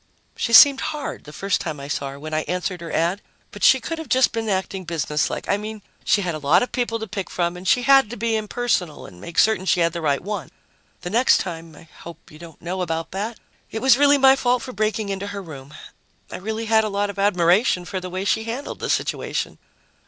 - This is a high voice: Yes, high, 195 Hz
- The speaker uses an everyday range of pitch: Yes, average, 4.8 semitones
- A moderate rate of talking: No, fast, 240 wpm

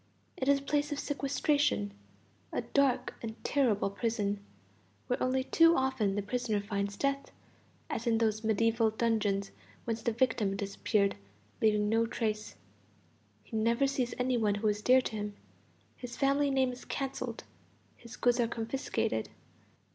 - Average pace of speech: Yes, average, 145 wpm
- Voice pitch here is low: No, high, 230 Hz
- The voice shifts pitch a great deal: No, average, 3.8 semitones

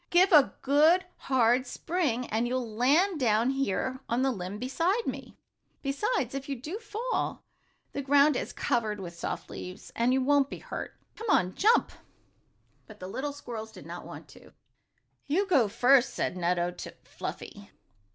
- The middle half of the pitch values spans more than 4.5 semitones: Yes, average, 5.1 semitones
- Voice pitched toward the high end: Yes, very high, 265 Hz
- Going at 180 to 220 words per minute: No, average, 165 wpm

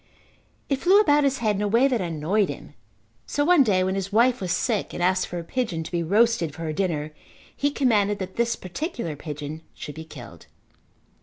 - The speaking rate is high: Yes, fast, 210 wpm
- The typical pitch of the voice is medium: No, high, 200 Hz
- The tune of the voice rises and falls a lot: Yes, wide, 6.8 semitones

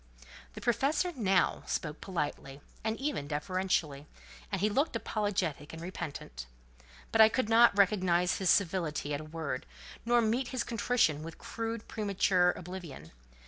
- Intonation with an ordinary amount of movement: No, wide, 6.0 semitones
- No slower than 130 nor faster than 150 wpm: Yes, average, 145 wpm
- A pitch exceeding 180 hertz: Yes, high, 190 Hz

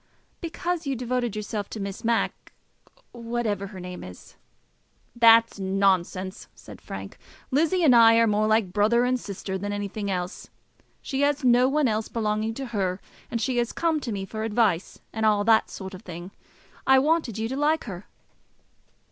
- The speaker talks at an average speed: Yes, average, 175 wpm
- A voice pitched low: No, high, 220 Hz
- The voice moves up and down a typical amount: Yes, average, 4.0 semitones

